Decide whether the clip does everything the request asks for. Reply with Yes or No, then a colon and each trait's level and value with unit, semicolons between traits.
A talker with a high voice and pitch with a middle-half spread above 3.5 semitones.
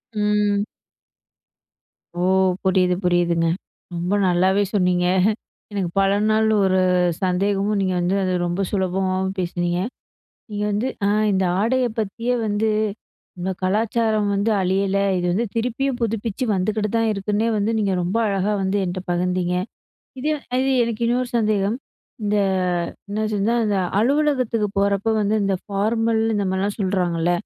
No: high, 200 Hz; average, 2.8 semitones